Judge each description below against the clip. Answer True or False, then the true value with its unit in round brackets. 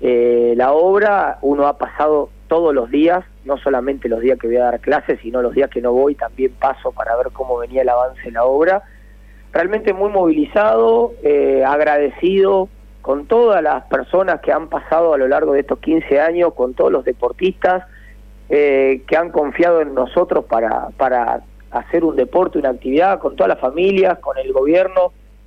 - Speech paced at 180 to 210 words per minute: True (185 wpm)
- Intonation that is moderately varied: False (6.3 semitones)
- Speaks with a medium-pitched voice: True (145 Hz)